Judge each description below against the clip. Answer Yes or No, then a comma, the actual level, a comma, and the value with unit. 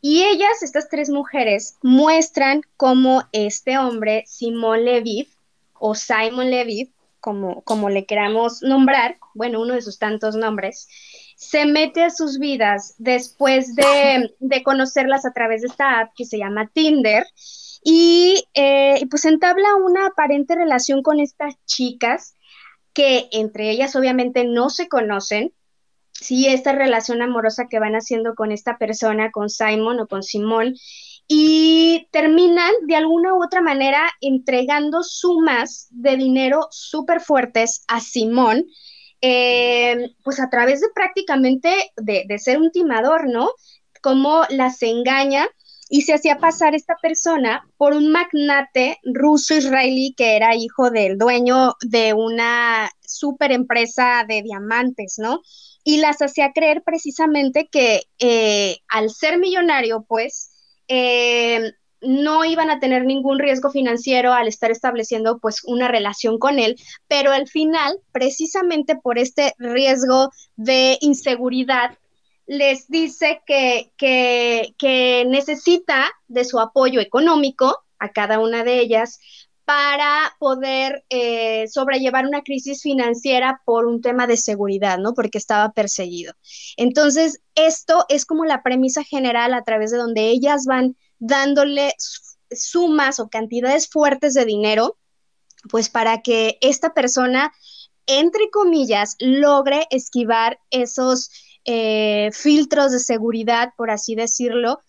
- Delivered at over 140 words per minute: No, average, 135 wpm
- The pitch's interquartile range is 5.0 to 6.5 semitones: No, average, 4.1 semitones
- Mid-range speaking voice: No, very high, 260 Hz